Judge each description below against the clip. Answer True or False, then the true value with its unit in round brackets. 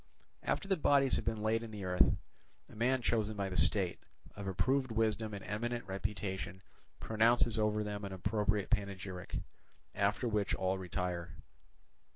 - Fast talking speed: False (155 wpm)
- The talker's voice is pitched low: True (105 Hz)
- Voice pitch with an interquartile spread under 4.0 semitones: True (2.9 semitones)